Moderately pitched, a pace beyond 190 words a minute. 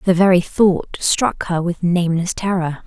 No: medium, 180 Hz; average, 170 wpm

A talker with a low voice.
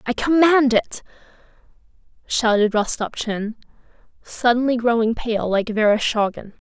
No: high, 230 Hz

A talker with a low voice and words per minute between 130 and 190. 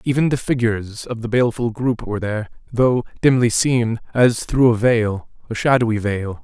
Yes: low, 115 Hz; average, 170 wpm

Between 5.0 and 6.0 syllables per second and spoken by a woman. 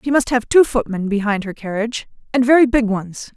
Yes: 5.7 syllables/s; female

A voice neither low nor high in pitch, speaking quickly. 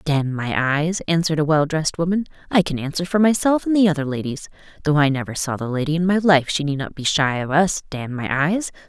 Yes: medium, 155 Hz; fast, 245 wpm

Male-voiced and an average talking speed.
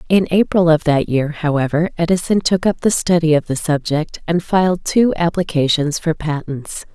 No: female; average, 175 wpm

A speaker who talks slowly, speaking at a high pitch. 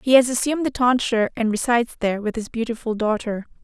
No: average, 200 wpm; high, 235 Hz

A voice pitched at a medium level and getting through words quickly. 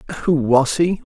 No: medium, 150 Hz; average, 165 wpm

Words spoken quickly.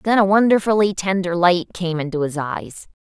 No: average, 180 wpm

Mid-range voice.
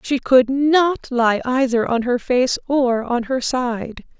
No: very high, 250 Hz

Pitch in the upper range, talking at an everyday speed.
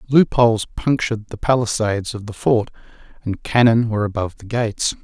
No: low, 110 Hz; average, 165 wpm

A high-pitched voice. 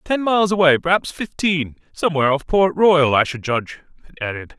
No: medium, 160 Hz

